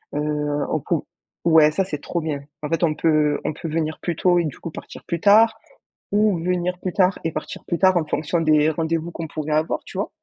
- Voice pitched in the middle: Yes, medium, 165 Hz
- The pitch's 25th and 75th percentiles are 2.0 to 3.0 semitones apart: Yes, narrow, 2.5 semitones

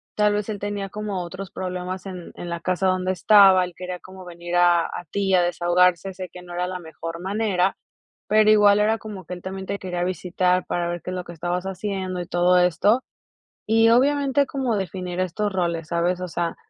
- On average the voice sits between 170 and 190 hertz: Yes, medium, 185 Hz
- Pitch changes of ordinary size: No, narrow, 2.3 semitones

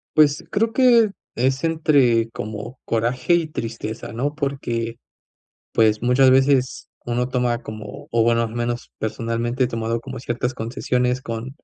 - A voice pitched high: No, low, 125 Hz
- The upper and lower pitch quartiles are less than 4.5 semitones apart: Yes, average, 2.8 semitones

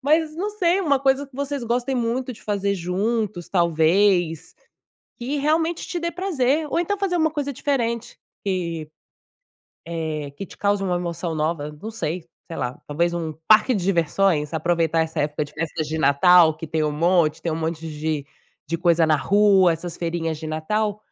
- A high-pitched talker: No, medium, 180 Hz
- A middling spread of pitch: No, wide, 7.5 semitones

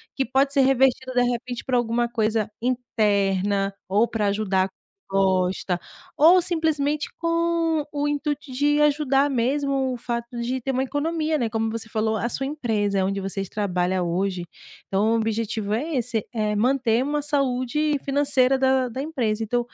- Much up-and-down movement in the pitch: No, average, 4.7 semitones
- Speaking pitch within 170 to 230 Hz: No, high, 245 Hz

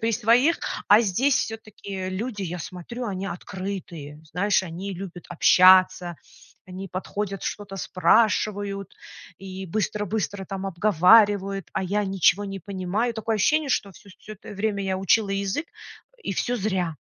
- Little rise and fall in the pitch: Yes, narrow, 2.3 semitones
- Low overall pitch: No, high, 195 Hz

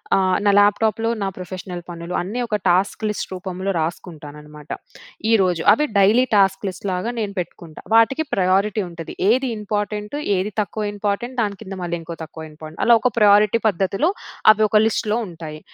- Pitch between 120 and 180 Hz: No, high, 195 Hz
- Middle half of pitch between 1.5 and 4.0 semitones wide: Yes, average, 3.3 semitones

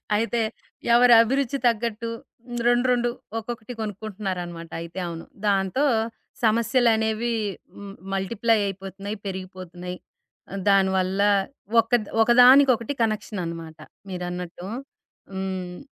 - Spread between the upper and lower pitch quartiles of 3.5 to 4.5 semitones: Yes, average, 3.9 semitones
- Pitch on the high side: Yes, high, 205 Hz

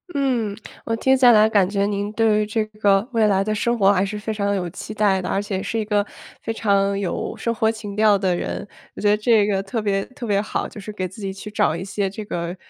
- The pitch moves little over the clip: Yes, narrow, 1.7 semitones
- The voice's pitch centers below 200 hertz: No, high, 205 Hz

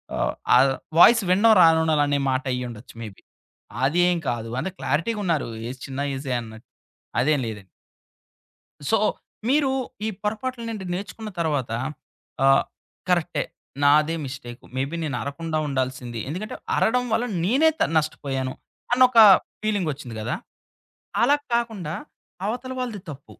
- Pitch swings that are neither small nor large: No, wide, 8.4 semitones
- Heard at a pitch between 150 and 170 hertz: Yes, medium, 155 Hz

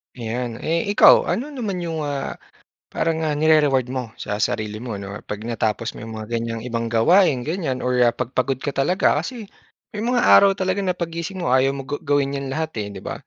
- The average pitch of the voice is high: No, low, 135 Hz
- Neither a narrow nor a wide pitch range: No, wide, 6.4 semitones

